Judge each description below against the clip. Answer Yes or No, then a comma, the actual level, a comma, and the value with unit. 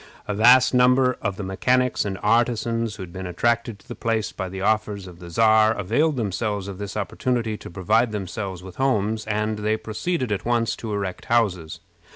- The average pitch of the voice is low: Yes, low, 110 Hz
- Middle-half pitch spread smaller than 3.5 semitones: Yes, average, 3.0 semitones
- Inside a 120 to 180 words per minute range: No, average, 190 wpm